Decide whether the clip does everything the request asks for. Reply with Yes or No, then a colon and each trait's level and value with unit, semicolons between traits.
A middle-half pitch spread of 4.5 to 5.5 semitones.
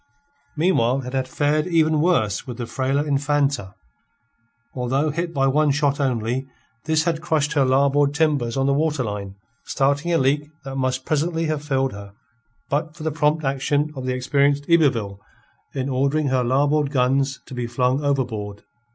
No: average, 2.7 semitones